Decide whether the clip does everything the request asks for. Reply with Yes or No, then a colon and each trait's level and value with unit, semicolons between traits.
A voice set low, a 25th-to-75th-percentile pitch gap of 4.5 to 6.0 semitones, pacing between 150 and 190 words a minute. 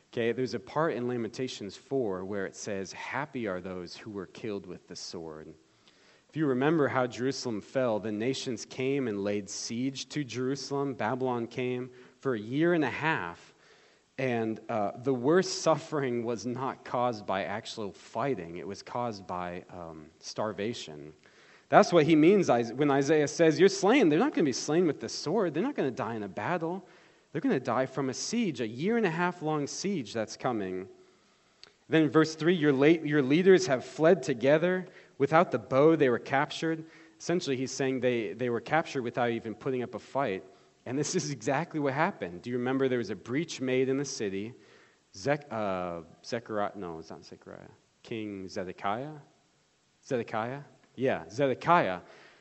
Yes: low, 130 Hz; average, 5.2 semitones; average, 180 wpm